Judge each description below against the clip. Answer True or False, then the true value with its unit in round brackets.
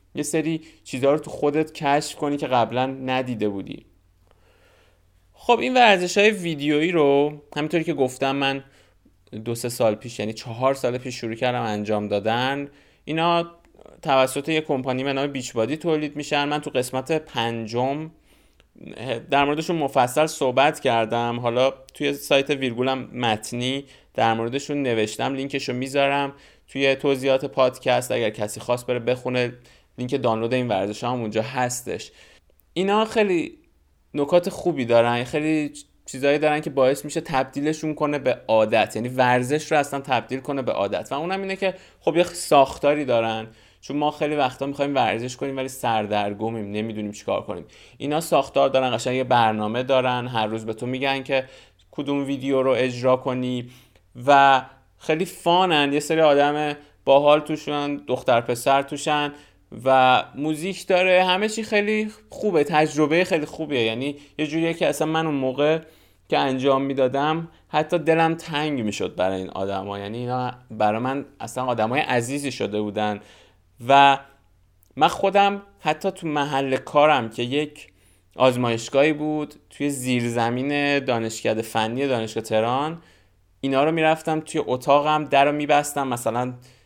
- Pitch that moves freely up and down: False (3.8 semitones)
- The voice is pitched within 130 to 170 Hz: True (135 Hz)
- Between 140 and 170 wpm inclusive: True (145 wpm)